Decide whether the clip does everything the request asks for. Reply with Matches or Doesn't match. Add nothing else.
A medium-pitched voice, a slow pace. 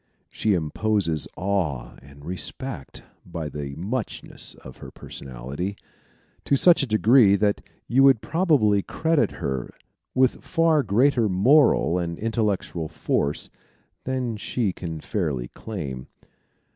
Doesn't match